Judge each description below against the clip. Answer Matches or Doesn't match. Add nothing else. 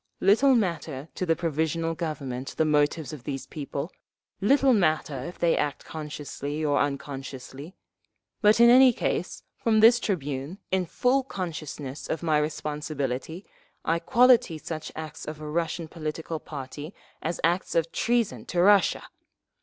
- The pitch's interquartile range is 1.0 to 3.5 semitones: Doesn't match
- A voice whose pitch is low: Doesn't match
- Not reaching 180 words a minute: Matches